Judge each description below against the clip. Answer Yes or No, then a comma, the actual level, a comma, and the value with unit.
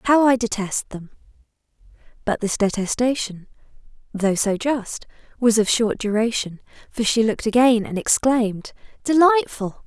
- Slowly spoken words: Yes, slow, 130 wpm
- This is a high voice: Yes, high, 225 Hz